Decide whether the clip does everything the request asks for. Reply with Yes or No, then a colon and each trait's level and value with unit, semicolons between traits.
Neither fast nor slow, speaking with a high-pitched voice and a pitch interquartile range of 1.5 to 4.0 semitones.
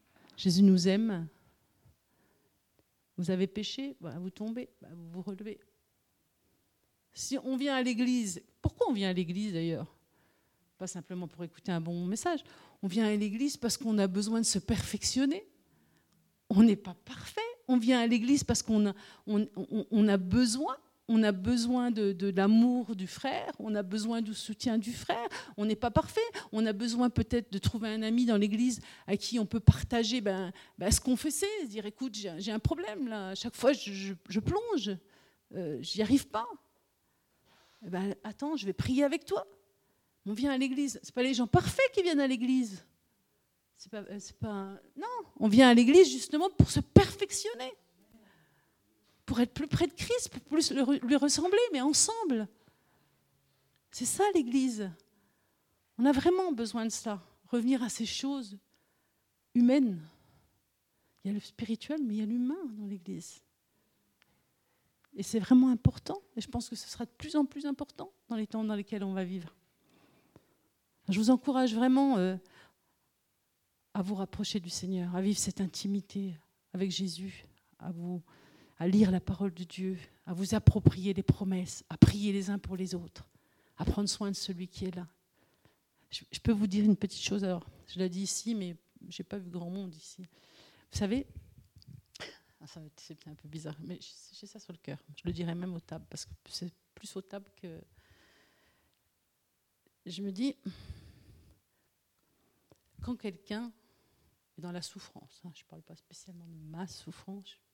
No: average, 175 wpm; high, 210 Hz; average, 5.1 semitones